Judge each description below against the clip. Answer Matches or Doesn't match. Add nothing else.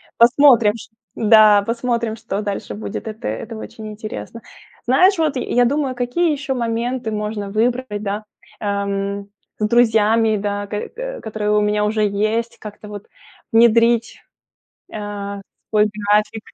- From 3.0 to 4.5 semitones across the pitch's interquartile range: Doesn't match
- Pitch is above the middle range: Matches